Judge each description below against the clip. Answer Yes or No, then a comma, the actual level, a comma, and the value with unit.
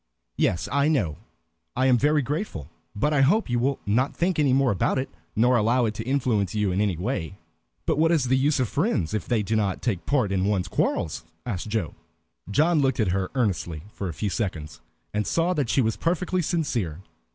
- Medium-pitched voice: No, low, 120 Hz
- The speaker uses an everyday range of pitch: No, wide, 6.2 semitones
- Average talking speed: No, fast, 215 wpm